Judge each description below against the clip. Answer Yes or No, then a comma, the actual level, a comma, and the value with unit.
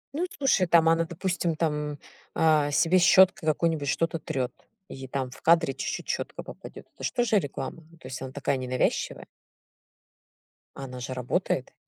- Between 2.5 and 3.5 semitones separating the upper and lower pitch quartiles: No, average, 4.1 semitones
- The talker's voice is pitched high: No, medium, 160 Hz